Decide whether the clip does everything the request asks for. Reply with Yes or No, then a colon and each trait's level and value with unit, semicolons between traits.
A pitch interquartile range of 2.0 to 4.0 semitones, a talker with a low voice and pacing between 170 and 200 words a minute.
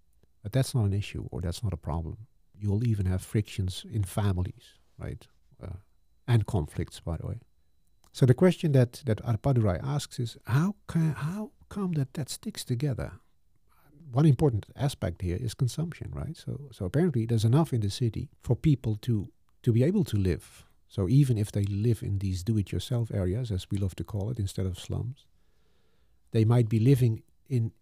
No: average, 5.1 semitones; low, 115 Hz; average, 185 wpm